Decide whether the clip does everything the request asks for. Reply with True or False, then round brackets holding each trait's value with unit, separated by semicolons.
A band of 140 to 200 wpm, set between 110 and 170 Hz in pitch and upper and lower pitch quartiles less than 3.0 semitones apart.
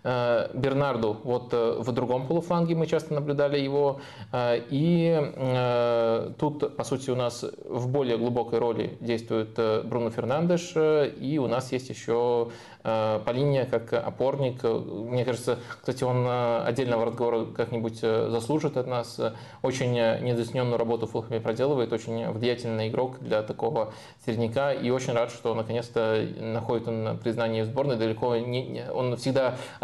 False (130 wpm; 120 Hz; 2.4 semitones)